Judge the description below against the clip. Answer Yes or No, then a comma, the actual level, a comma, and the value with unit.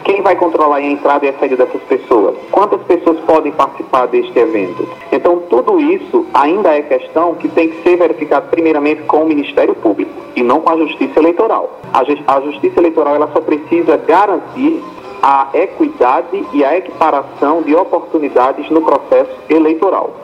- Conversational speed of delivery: Yes, average, 165 wpm